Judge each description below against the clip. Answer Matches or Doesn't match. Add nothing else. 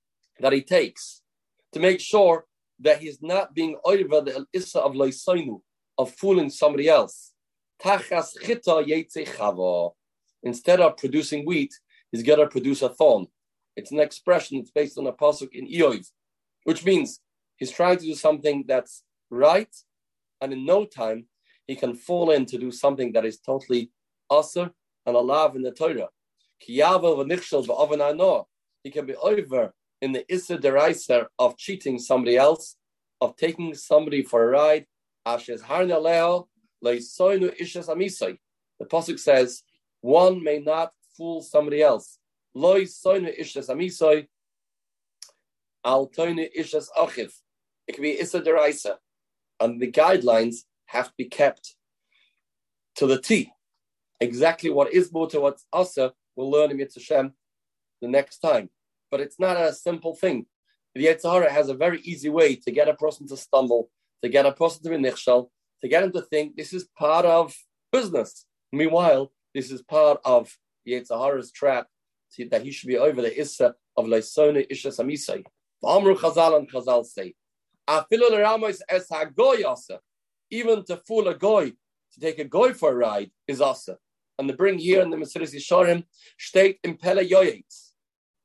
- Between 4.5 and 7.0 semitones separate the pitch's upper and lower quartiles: Matches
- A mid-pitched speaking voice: Matches